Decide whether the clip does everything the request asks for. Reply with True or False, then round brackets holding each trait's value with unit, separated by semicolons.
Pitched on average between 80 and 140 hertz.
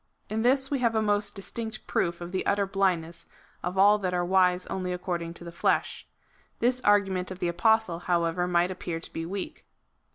False (185 Hz)